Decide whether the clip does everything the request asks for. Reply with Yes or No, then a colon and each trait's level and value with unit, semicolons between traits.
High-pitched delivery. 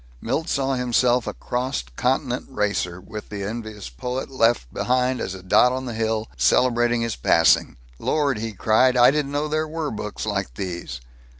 No: low, 120 Hz